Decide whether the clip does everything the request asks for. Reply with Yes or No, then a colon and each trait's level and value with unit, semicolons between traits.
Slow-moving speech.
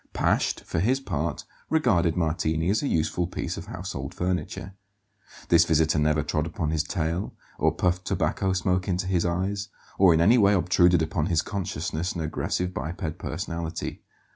No: average, 165 wpm